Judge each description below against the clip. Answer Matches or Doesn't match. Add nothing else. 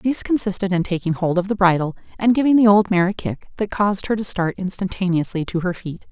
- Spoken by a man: Doesn't match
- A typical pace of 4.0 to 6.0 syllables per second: Doesn't match